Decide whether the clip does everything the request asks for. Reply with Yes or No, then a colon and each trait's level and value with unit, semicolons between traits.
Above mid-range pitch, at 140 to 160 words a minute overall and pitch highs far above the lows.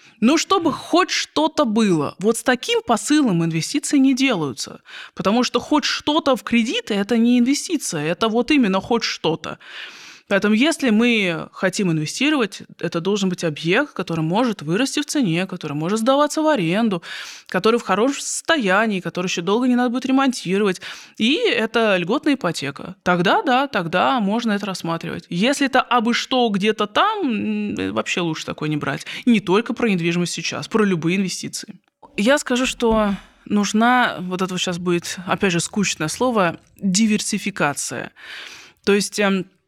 Yes: high, 215 Hz; average, 155 wpm; wide, 5.7 semitones